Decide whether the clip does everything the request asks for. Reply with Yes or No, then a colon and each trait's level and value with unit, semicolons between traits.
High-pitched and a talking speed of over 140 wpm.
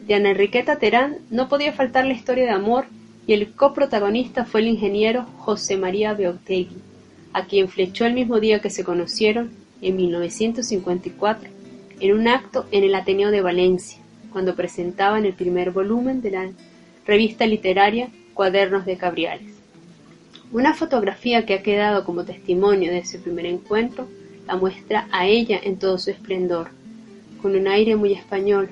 Yes: high, 205 Hz; average, 155 wpm